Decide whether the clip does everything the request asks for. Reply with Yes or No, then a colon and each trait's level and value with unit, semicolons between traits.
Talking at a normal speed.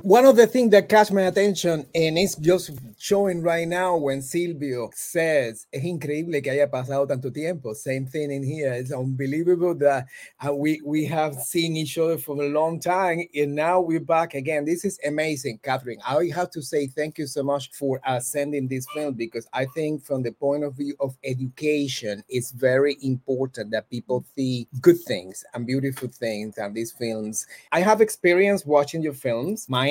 Yes: average, 185 wpm